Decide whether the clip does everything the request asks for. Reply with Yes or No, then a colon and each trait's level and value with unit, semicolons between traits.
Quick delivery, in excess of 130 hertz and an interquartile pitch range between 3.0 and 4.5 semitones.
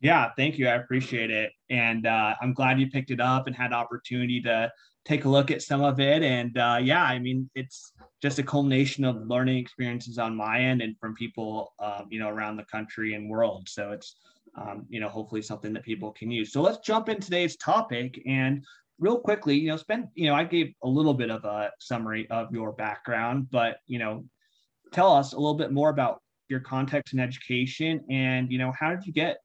No: fast, 220 wpm; low, 125 Hz; average, 3.7 semitones